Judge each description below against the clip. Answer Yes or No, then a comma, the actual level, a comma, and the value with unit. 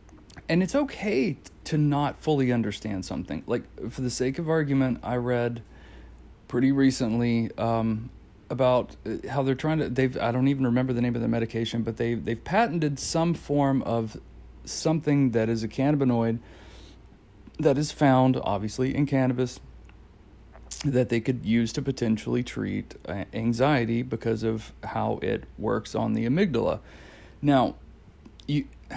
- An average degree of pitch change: Yes, average, 3.3 semitones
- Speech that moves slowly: No, average, 145 wpm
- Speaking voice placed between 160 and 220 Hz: No, low, 125 Hz